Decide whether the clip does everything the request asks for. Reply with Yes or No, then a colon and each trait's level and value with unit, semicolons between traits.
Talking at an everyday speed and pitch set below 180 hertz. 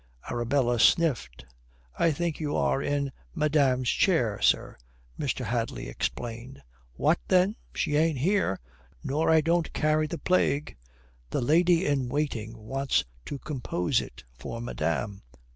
No: slow, 130 wpm; medium, 140 Hz